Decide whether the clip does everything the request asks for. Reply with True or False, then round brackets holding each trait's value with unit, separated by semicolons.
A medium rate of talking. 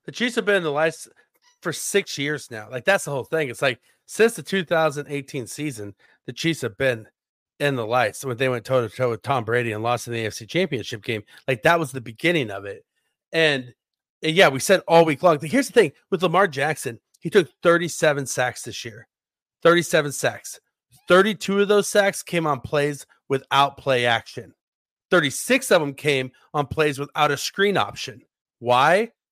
True (195 wpm)